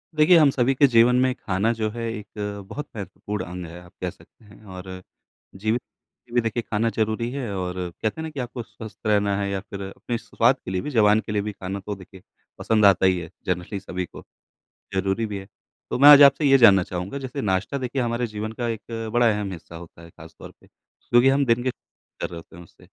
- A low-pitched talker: Yes, low, 105 Hz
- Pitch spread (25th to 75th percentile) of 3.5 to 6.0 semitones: Yes, average, 4.1 semitones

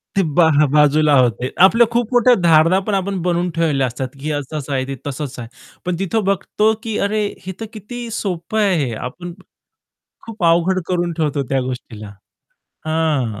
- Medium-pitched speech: Yes, medium, 170 Hz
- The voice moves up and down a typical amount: No, wide, 5.9 semitones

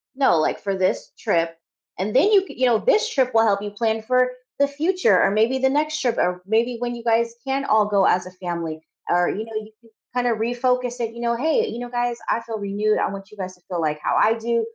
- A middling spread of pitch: Yes, average, 4.1 semitones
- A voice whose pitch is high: Yes, high, 230 Hz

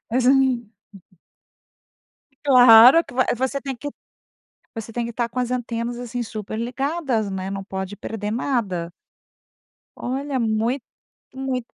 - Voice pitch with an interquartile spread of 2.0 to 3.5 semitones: Yes, average, 3.0 semitones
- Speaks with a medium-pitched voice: No, high, 240 Hz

